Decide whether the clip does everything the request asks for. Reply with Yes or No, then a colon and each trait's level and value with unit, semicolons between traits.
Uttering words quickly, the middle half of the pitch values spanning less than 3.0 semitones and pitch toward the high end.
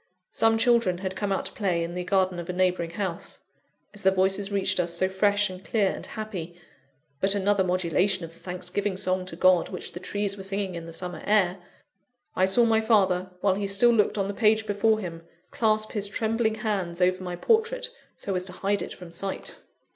Yes: fast, 210 wpm; narrow, 2.4 semitones; high, 195 Hz